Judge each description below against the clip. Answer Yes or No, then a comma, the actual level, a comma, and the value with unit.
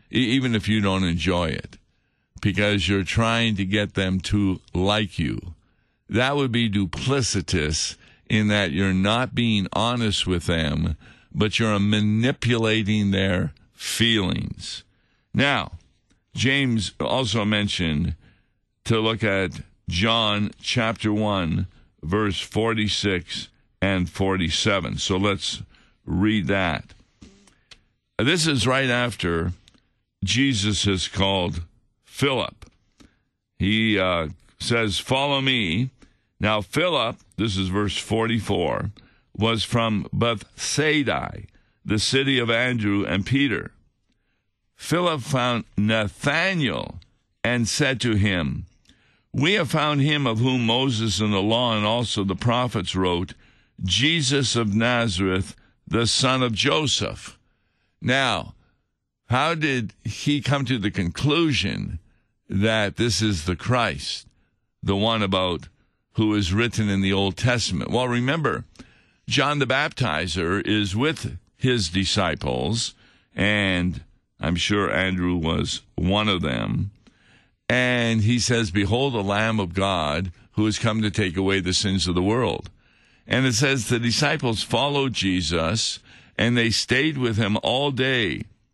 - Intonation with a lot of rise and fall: No, average, 3.9 semitones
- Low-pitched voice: Yes, low, 105 Hz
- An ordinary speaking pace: No, slow, 120 wpm